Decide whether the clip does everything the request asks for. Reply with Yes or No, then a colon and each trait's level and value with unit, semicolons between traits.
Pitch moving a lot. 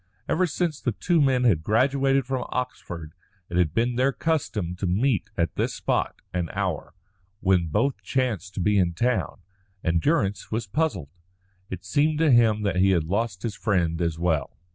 Yes: wide, 6.7 semitones